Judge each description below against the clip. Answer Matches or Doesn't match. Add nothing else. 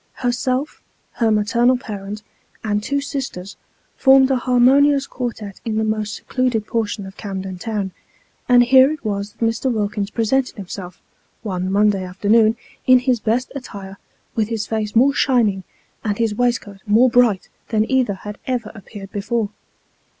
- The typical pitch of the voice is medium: Doesn't match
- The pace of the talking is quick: Doesn't match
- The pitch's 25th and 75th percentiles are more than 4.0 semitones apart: Doesn't match